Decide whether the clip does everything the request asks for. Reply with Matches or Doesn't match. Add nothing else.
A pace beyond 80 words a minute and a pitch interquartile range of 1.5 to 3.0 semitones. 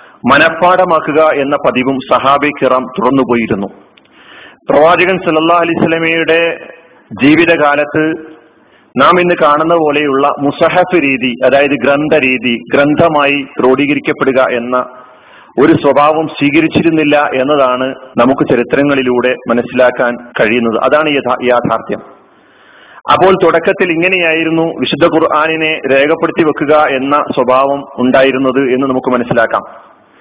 Doesn't match